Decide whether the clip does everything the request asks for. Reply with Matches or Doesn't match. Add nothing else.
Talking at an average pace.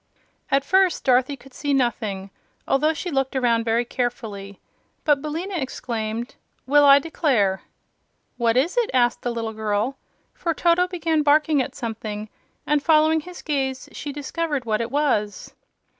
Matches